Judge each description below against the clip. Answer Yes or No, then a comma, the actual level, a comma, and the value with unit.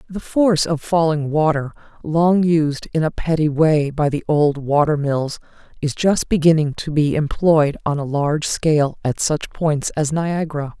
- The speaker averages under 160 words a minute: No, average, 170 wpm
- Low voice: No, medium, 155 Hz